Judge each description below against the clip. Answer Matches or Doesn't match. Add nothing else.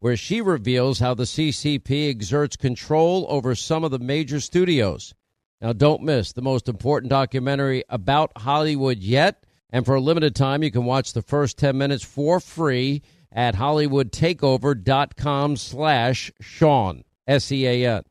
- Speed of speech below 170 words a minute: Matches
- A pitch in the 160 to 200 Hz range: Doesn't match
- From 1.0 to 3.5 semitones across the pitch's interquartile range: Matches